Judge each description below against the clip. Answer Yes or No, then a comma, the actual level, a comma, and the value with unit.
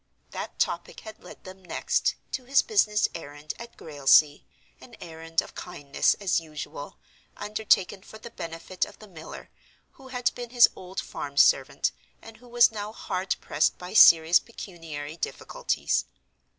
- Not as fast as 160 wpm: Yes, average, 150 wpm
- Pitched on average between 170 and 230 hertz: Yes, medium, 185 Hz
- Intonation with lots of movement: Yes, wide, 5.8 semitones